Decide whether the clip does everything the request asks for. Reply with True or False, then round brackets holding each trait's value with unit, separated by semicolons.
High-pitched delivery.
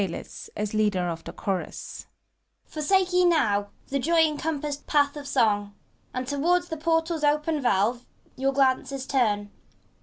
True (275 Hz)